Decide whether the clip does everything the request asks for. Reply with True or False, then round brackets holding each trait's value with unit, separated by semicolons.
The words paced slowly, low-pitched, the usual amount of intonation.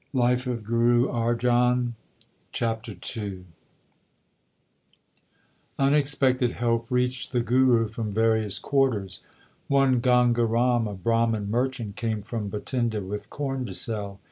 False (115 wpm; 120 Hz; 2.2 semitones)